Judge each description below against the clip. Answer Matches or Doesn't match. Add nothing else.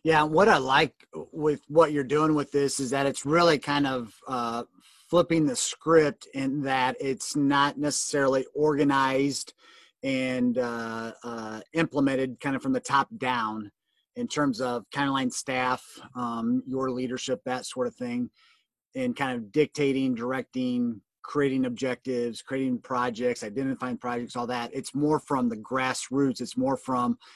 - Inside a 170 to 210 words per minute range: Doesn't match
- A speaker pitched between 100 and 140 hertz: Matches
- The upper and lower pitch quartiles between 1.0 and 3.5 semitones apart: Matches